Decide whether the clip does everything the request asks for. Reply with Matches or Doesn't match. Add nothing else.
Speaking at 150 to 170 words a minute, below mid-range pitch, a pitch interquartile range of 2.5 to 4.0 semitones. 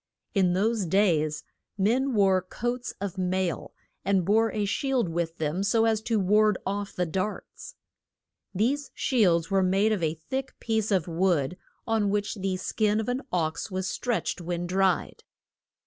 Doesn't match